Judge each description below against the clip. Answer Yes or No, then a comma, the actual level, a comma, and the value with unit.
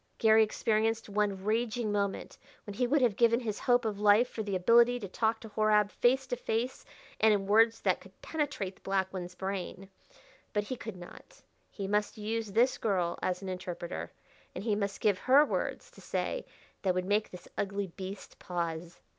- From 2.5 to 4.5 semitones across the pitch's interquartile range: Yes, average, 2.9 semitones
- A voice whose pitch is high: Yes, high, 210 Hz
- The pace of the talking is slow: No, average, 190 wpm